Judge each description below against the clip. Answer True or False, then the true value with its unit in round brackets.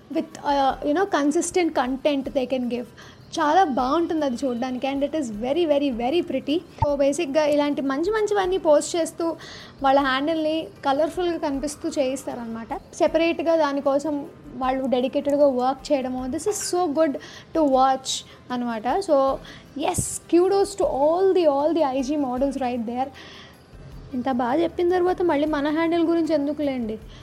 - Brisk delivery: True (140 wpm)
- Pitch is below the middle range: False (295 Hz)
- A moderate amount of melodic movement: True (3.3 semitones)